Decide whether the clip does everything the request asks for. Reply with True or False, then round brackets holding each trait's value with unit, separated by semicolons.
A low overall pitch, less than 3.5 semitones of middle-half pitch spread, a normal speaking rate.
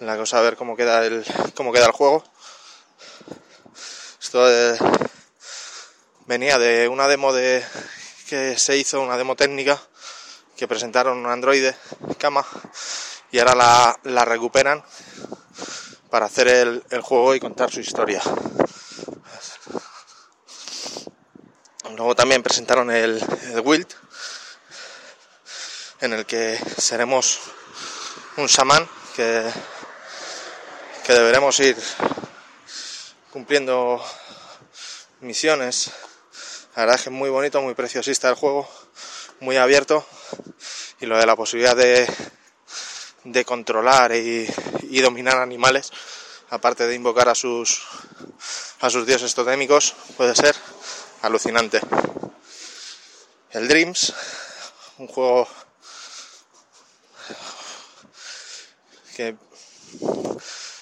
False (130 Hz; 2.9 semitones; 100 wpm)